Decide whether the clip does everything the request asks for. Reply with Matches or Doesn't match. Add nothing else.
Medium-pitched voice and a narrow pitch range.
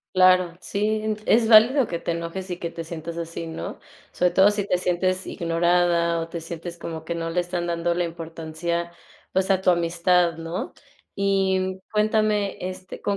Matches